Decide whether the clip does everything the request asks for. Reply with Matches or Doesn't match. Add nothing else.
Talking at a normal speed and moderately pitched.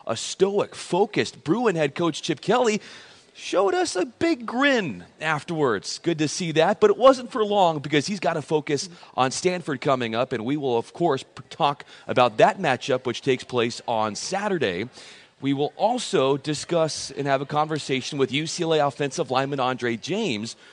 Matches